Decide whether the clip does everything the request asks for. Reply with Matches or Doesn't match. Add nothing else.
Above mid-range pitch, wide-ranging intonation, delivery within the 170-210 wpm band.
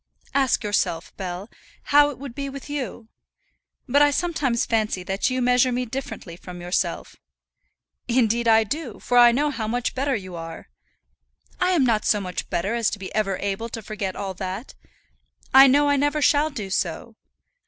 Matches